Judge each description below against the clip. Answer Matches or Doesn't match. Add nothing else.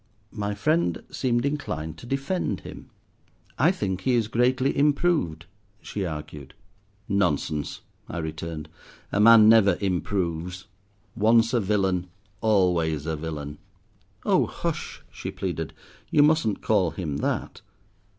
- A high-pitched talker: Doesn't match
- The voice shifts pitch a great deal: Matches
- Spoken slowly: Matches